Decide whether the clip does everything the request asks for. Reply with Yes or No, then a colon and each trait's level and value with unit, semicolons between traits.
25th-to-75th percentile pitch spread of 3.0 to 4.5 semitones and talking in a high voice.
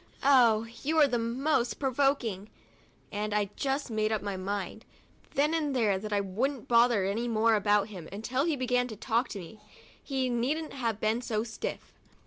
Yes: average, 4.0 semitones; high, 230 Hz